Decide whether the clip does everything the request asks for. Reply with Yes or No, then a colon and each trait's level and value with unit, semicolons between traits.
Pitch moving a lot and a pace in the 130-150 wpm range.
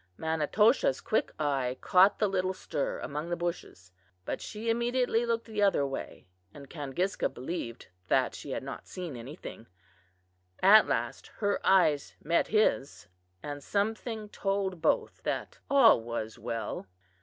Yes: wide, 7.1 semitones; average, 140 wpm